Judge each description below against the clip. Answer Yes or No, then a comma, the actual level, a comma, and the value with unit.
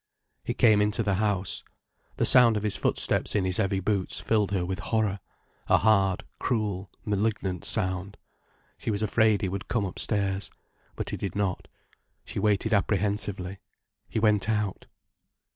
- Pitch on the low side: Yes, low, 100 Hz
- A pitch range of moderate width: No, narrow, 1.9 semitones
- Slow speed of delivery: No, average, 155 wpm